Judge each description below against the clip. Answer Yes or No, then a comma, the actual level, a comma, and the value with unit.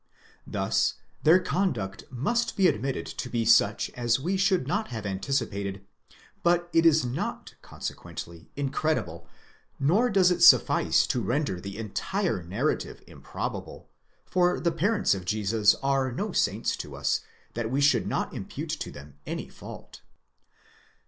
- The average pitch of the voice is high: No, low, 135 Hz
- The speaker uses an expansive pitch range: Yes, wide, 8.9 semitones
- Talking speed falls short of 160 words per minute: Yes, average, 140 wpm